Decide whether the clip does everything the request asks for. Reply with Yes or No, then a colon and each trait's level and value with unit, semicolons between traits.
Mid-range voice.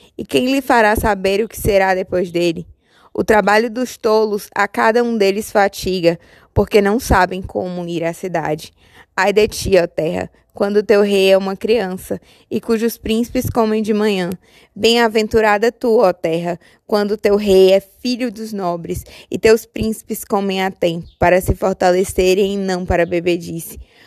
No: high, 200 Hz